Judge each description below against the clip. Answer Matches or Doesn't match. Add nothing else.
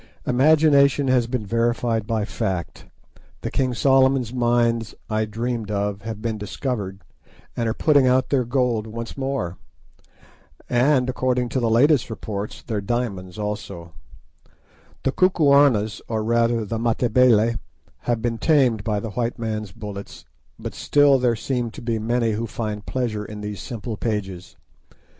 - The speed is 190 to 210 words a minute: Doesn't match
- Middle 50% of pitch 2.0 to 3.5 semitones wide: Matches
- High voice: Doesn't match